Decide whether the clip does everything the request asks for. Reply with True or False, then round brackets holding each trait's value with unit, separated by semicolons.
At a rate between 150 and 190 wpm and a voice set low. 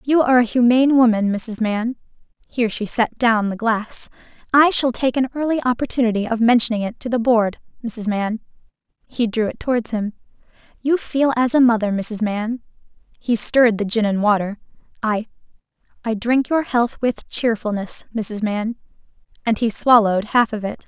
False (170 wpm; 230 Hz)